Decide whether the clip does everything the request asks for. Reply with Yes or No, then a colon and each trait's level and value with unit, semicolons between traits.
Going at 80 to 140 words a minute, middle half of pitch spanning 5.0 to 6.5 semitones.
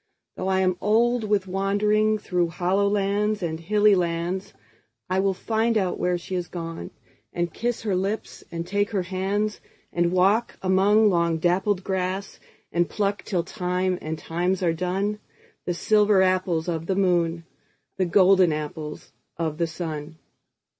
No: slow, 135 wpm; average, 2.9 semitones